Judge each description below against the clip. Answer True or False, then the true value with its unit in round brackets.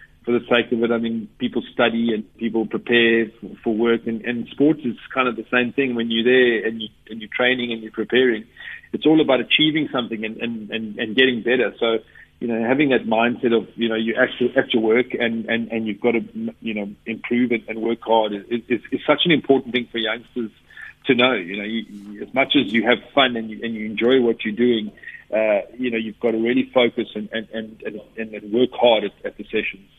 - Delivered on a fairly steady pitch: True (1.6 semitones)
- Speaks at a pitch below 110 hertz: False (115 Hz)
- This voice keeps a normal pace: False (240 wpm)